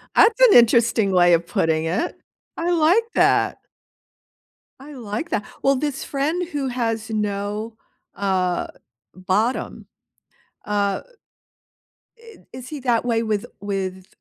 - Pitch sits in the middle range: No, high, 225 Hz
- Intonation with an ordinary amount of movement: No, wide, 5.7 semitones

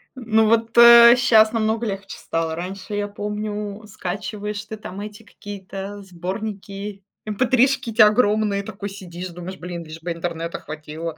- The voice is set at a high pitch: Yes, high, 205 Hz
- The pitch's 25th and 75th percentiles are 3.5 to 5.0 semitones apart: No, average, 3.0 semitones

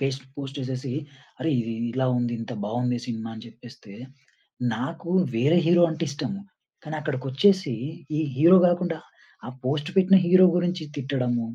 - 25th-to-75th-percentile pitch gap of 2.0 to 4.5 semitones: No, average, 5.0 semitones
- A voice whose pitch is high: No, low, 135 Hz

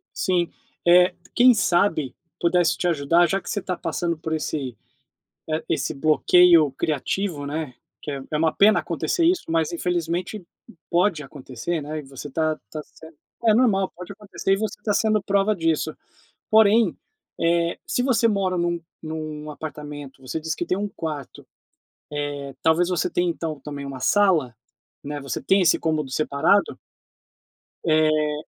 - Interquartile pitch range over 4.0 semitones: No, average, 3.7 semitones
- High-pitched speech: No, medium, 165 Hz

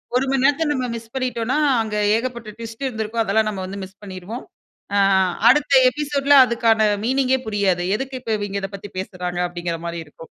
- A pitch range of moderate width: Yes, average, 4.7 semitones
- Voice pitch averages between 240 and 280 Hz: No, high, 225 Hz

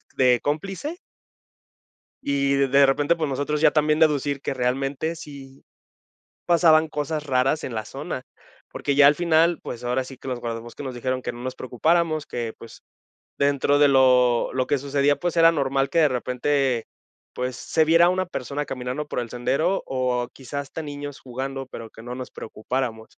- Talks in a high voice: No, medium, 140 Hz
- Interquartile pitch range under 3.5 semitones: Yes, average, 3.0 semitones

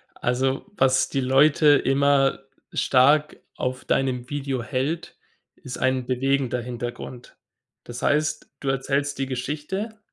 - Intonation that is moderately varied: No, narrow, 2.0 semitones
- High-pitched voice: No, low, 135 Hz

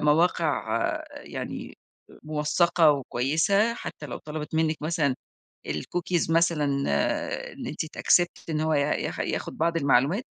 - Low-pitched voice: No, medium, 155 Hz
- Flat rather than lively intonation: Yes, narrow, 2.2 semitones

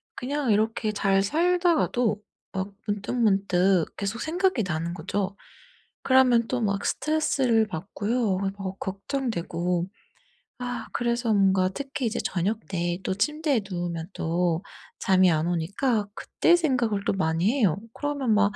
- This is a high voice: Yes, high, 205 Hz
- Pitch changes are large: No, average, 4.9 semitones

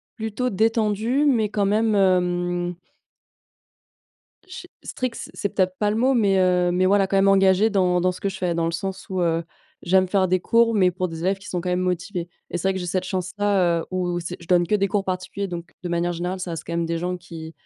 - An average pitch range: No, narrow, 2.3 semitones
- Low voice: No, medium, 185 Hz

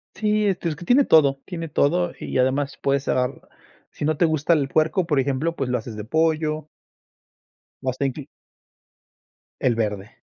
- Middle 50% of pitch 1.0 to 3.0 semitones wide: No, average, 4.0 semitones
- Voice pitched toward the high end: No, medium, 150 Hz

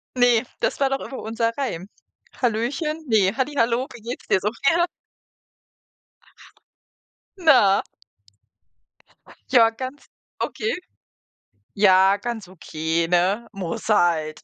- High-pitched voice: Yes, high, 225 Hz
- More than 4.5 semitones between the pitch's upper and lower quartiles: Yes, wide, 5.4 semitones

